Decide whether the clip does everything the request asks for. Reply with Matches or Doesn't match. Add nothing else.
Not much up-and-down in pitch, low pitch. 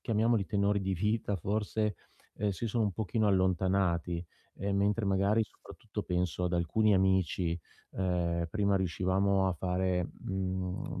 Matches